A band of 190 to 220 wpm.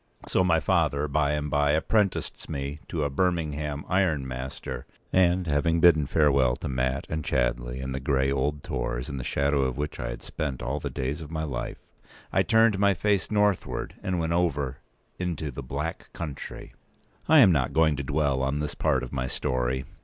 Yes: average, 195 wpm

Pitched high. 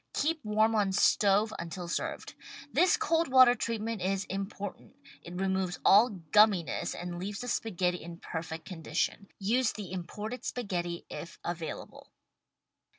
Yes: high, 195 Hz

